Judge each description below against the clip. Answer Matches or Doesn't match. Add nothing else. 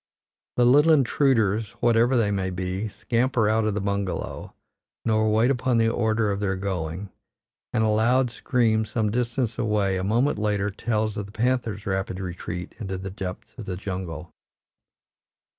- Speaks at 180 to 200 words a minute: Doesn't match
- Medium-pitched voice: Doesn't match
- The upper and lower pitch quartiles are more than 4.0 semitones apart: Doesn't match